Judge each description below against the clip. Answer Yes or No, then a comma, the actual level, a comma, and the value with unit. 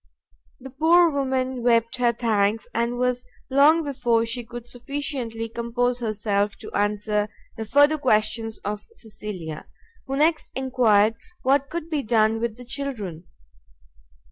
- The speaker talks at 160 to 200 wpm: No, slow, 135 wpm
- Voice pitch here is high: Yes, high, 235 Hz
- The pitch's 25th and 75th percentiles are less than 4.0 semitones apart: Yes, average, 3.6 semitones